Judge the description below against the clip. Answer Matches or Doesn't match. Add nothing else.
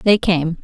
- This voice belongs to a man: Doesn't match